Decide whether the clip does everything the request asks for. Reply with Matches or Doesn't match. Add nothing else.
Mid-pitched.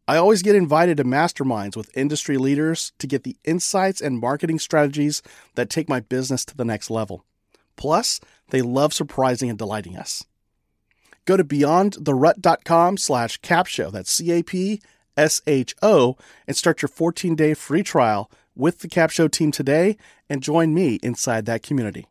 Matches